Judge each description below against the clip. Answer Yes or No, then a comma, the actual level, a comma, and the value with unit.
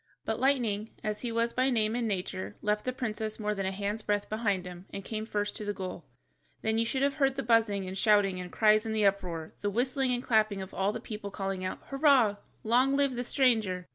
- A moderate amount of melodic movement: Yes, average, 3.3 semitones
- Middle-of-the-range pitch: No, high, 215 Hz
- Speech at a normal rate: No, fast, 230 wpm